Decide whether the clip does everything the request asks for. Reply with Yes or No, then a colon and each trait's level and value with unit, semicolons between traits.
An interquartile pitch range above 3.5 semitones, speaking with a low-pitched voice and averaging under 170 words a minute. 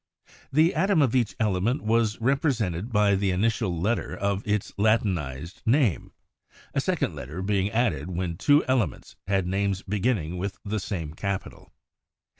Yes: average, 4.0 semitones; low, 100 Hz; average, 145 wpm